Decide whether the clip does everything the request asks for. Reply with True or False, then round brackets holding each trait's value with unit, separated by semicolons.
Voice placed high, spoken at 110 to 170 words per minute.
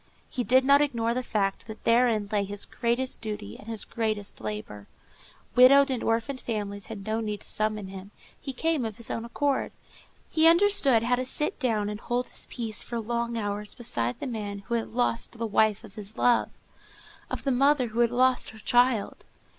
False (230 Hz; 195 wpm)